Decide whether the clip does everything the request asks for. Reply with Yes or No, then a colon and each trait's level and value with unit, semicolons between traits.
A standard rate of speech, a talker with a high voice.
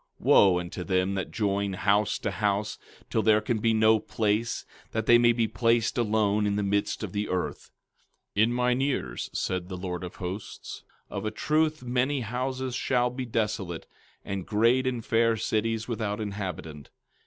No: average, 175 wpm; low, 110 Hz